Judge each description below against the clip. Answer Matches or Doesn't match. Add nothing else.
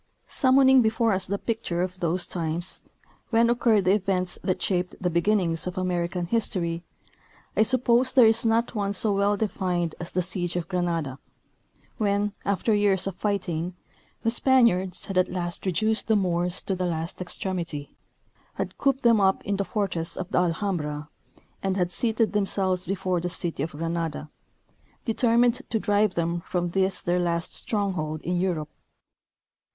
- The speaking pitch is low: Doesn't match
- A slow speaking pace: Doesn't match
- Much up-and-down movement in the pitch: Doesn't match